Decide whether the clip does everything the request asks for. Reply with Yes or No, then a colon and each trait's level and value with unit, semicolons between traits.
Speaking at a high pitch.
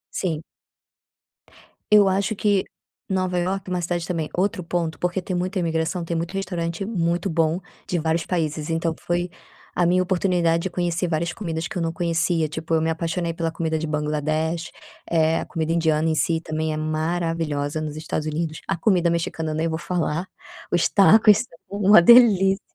No: medium, 170 Hz